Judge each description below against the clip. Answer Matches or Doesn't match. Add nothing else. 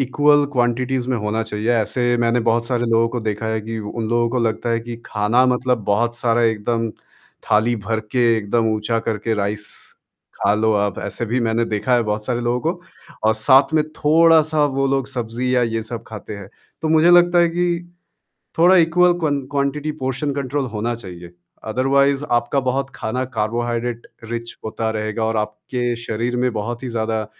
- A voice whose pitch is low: Matches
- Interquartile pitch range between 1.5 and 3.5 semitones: Matches